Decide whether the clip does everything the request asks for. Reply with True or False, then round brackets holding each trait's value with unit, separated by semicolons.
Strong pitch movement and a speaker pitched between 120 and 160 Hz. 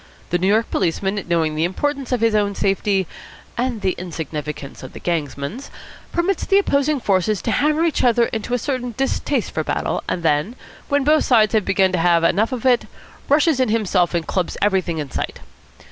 False (6.7 semitones; 210 Hz)